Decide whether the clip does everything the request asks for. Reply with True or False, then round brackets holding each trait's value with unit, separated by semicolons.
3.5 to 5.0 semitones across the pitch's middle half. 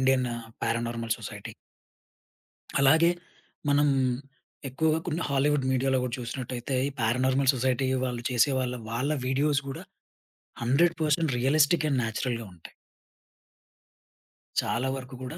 False (2.8 semitones)